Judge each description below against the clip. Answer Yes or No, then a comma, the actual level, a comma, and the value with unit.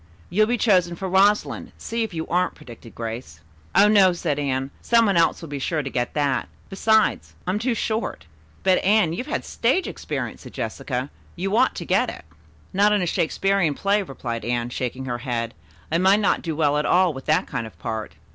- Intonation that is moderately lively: No, wide, 7.3 semitones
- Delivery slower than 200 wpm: No, fast, 205 wpm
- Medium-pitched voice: Yes, medium, 170 Hz